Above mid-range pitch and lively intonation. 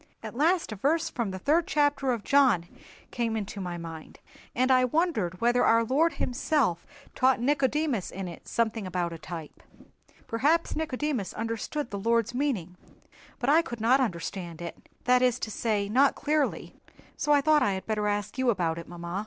Yes: high, 235 Hz; wide, 6.5 semitones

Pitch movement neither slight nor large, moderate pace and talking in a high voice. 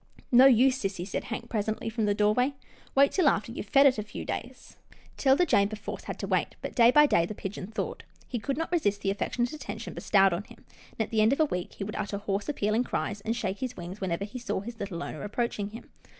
No: average, 4.0 semitones; fast, 255 wpm; high, 215 Hz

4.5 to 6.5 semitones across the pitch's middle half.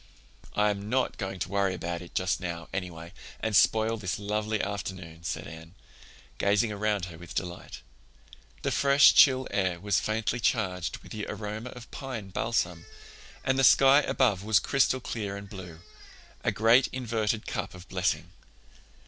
No: average, 3.7 semitones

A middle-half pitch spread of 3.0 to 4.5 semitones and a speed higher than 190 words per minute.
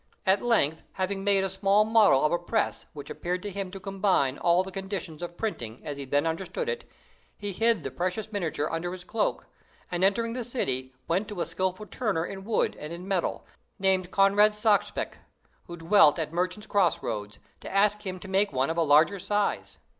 Yes: average, 3.8 semitones; average, 200 wpm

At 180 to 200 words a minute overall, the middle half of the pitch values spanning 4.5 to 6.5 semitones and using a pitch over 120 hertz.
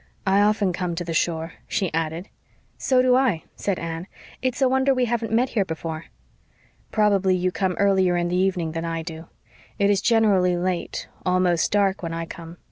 No: average, 190 wpm; average, 3.7 semitones; medium, 185 Hz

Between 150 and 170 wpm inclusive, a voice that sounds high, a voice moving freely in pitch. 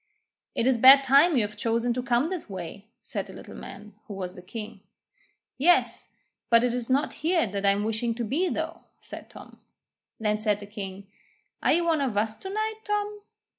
No: fast, 205 wpm; high, 235 Hz; wide, 6.7 semitones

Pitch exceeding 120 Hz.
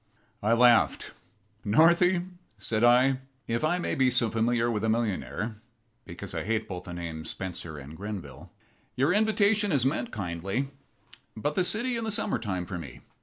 No: low, 115 Hz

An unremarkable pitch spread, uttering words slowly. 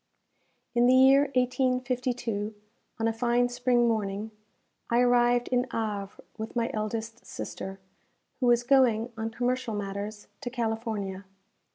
No: narrow, 2.3 semitones; slow, 130 wpm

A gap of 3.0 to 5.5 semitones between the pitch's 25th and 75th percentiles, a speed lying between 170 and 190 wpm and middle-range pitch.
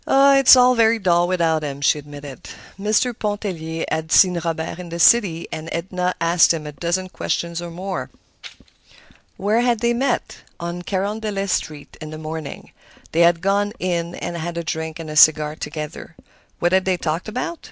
Yes: average, 4.0 semitones; average, 175 wpm; medium, 175 Hz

